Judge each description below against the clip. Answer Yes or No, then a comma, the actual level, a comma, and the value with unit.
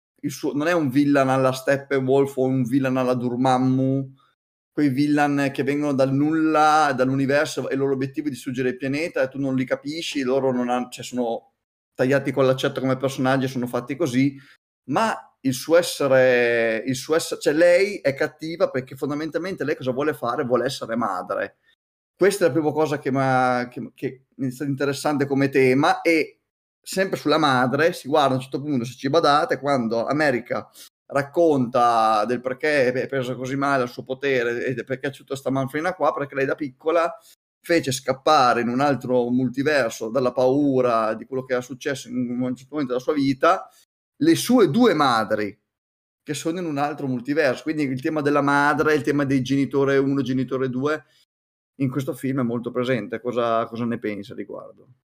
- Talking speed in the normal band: No, fast, 185 wpm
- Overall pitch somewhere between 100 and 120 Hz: No, low, 135 Hz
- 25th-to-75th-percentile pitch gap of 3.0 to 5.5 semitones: No, narrow, 2.5 semitones